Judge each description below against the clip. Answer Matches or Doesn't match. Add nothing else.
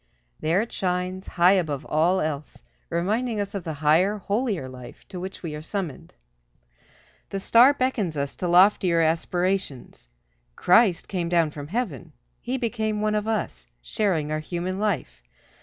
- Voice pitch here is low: Doesn't match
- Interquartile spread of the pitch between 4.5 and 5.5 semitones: Matches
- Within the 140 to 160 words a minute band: Matches